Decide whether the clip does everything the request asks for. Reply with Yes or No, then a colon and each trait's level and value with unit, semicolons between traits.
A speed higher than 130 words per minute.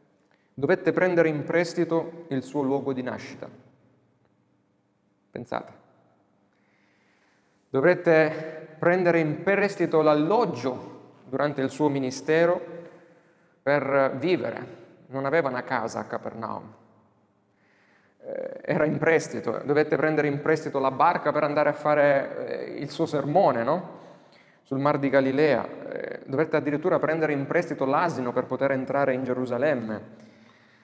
No: slow, 115 wpm